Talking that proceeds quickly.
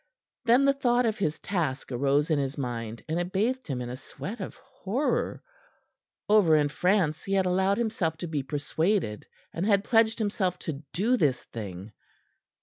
No: average, 175 wpm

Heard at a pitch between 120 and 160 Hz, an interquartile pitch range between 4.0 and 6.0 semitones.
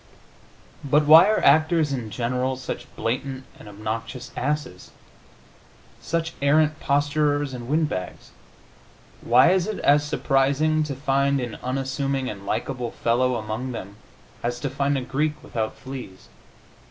No: low, 135 Hz; average, 3.4 semitones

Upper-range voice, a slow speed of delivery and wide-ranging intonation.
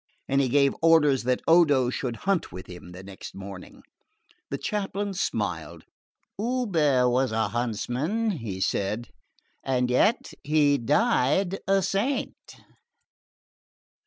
No: medium, 140 Hz; slow, 115 wpm; wide, 8.4 semitones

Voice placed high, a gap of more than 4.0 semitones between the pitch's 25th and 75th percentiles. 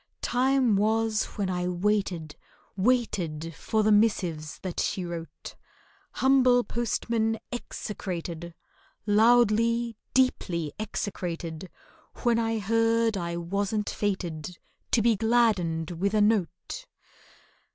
Yes: high, 210 Hz; average, 4.7 semitones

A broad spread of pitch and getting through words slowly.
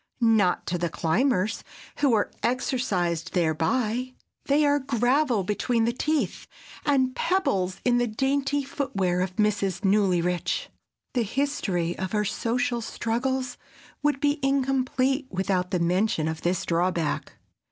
Yes: wide, 6.5 semitones; slow, 130 wpm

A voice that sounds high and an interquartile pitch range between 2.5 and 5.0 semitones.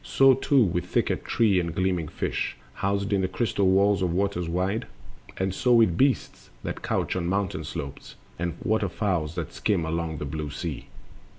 No: very low, 95 Hz; average, 3.2 semitones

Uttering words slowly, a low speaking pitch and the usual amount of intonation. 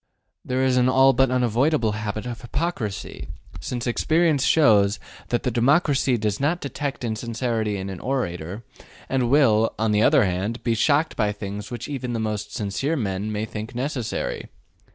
No: average, 165 wpm; low, 120 Hz; average, 3.9 semitones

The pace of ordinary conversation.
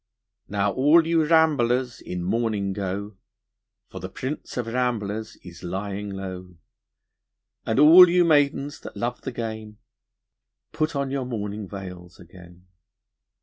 No: slow, 130 wpm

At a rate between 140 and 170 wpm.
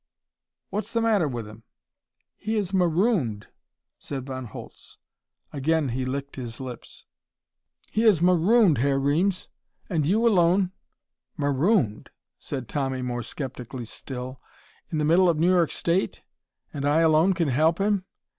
Yes: average, 145 wpm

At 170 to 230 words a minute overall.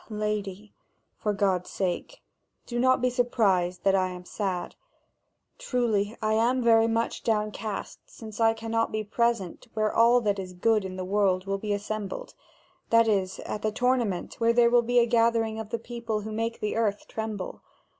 Yes: average, 180 wpm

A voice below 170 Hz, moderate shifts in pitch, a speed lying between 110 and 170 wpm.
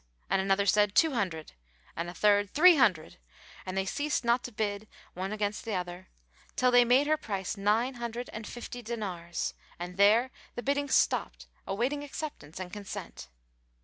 No: high, 210 Hz; average, 4.5 semitones; average, 165 wpm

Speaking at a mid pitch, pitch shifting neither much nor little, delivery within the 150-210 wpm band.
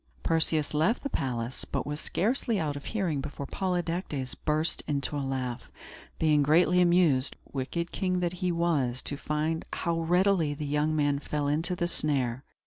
Yes: medium, 155 Hz; average, 3.4 semitones; average, 165 wpm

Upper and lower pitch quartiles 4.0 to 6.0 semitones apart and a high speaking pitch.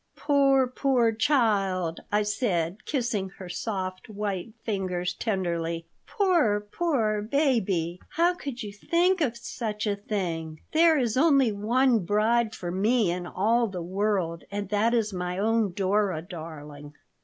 Yes: average, 4.6 semitones; high, 210 Hz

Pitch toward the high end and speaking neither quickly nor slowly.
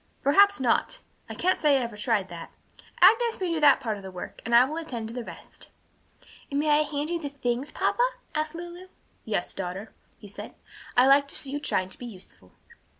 No: very high, 275 Hz; fast, 215 wpm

